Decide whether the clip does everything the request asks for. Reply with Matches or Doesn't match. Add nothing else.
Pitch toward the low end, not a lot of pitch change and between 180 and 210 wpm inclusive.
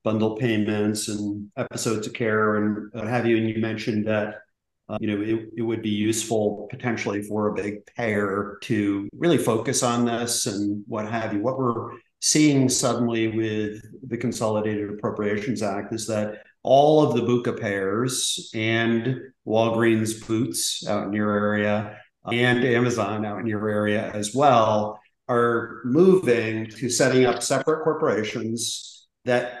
Doesn't match